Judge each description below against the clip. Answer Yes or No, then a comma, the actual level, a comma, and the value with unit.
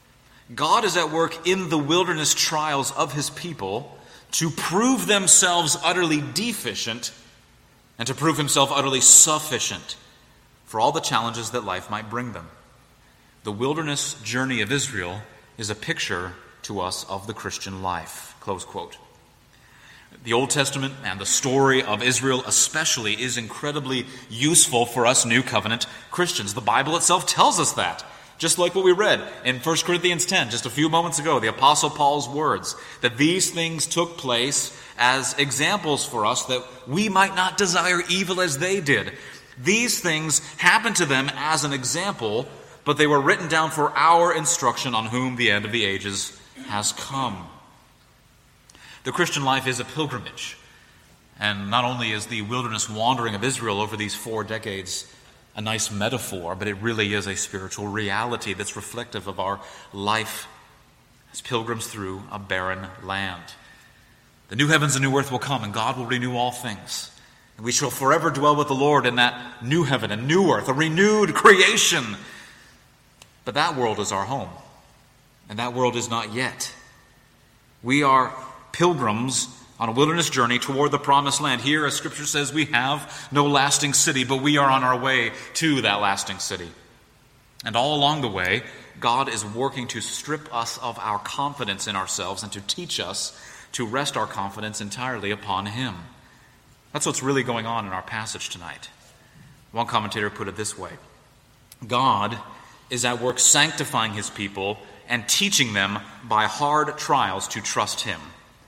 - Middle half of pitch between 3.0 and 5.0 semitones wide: No, wide, 5.6 semitones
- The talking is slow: No, average, 165 wpm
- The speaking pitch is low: Yes, low, 130 Hz